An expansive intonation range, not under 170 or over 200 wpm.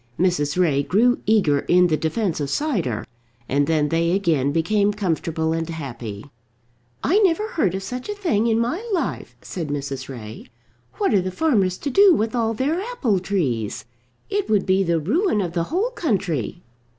Yes: wide, 7.2 semitones; average, 175 wpm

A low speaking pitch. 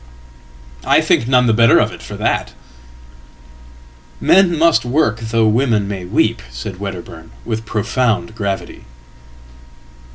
Yes: low, 100 Hz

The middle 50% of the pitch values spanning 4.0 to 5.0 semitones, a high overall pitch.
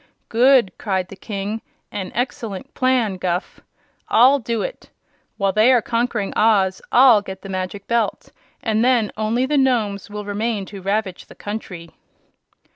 No: average, 3.3 semitones; high, 215 Hz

